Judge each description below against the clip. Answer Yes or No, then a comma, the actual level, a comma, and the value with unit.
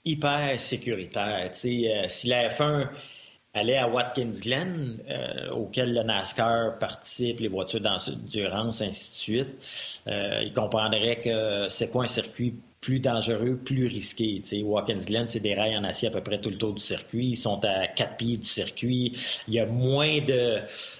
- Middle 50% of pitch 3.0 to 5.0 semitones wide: No, narrow, 2.5 semitones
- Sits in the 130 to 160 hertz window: No, low, 115 Hz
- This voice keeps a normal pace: Yes, average, 185 wpm